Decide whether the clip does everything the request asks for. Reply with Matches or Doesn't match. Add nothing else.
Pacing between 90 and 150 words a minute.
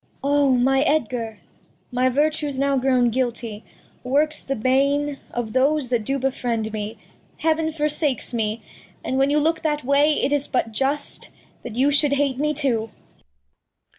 Doesn't match